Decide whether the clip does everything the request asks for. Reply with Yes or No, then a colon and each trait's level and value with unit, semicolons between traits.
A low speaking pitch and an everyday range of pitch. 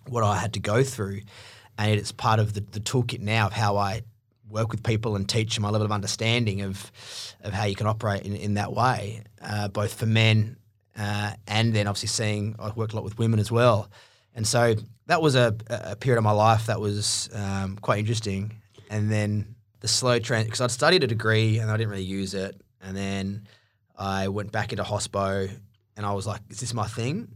No: low, 110 Hz; narrow, 1.6 semitones